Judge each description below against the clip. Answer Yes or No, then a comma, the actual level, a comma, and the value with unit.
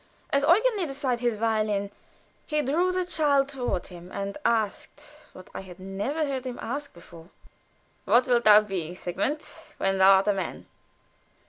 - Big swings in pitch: Yes, wide, 6.5 semitones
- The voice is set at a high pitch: Yes, high, 235 Hz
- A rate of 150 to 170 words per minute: Yes, average, 165 wpm